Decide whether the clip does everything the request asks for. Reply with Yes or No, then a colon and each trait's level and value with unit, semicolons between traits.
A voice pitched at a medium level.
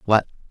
No: low, 110 Hz